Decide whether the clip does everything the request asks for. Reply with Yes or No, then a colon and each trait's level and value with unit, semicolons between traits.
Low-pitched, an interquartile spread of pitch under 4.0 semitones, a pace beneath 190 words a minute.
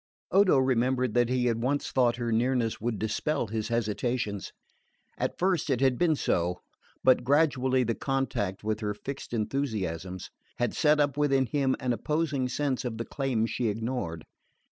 Yes: low, 125 Hz; average, 3.4 semitones; average, 160 wpm